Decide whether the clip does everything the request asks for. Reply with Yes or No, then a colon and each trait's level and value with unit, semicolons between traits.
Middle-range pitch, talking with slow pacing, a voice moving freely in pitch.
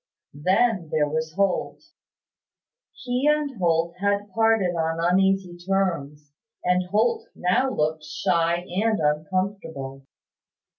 No: medium, 180 Hz; slow, 105 wpm; average, 4.2 semitones